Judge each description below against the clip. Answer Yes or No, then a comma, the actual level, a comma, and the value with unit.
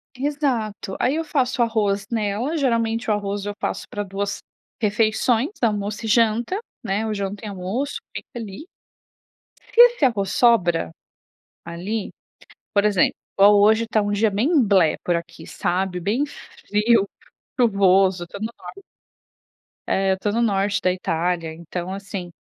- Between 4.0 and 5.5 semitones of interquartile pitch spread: No, average, 3.2 semitones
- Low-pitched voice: No, high, 205 Hz